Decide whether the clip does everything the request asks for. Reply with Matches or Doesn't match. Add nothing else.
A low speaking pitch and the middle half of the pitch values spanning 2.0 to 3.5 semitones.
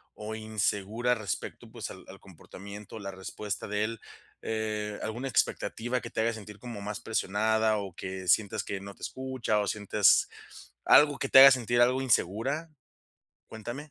Matches